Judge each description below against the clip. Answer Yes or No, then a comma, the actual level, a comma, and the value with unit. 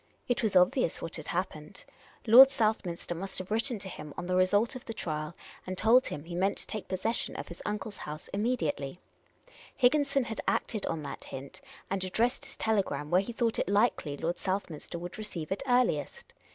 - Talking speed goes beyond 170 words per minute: Yes, average, 195 wpm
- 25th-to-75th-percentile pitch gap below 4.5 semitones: No, average, 5.1 semitones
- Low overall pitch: No, high, 195 Hz